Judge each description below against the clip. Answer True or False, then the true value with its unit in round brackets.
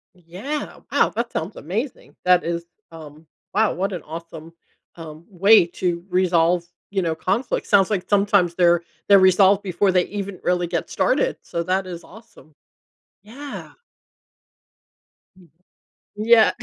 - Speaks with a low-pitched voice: False (180 Hz)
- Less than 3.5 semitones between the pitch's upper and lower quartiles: True (3.1 semitones)